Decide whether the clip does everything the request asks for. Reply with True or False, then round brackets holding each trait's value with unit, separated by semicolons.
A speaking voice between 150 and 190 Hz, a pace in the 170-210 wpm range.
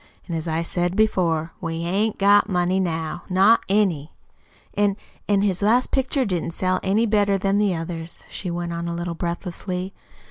True (185 Hz; 175 wpm)